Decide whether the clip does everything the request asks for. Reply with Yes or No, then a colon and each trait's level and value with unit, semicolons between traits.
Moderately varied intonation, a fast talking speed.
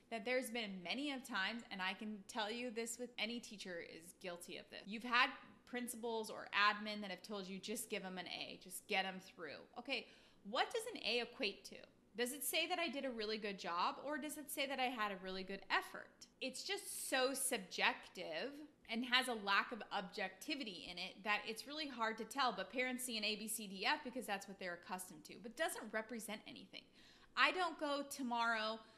Yes: average, 3.9 semitones; fast, 220 wpm